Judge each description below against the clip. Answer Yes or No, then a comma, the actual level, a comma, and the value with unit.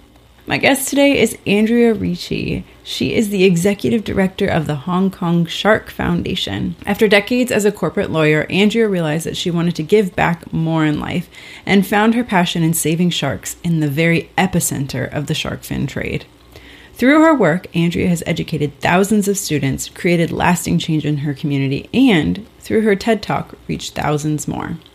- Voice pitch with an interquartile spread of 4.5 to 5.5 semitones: Yes, average, 5.2 semitones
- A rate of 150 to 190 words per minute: Yes, average, 175 wpm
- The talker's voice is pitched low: No, medium, 170 Hz